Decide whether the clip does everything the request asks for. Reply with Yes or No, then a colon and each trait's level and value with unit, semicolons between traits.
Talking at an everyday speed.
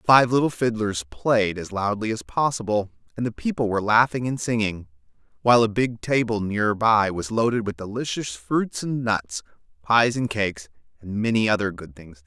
Yes: average, 185 wpm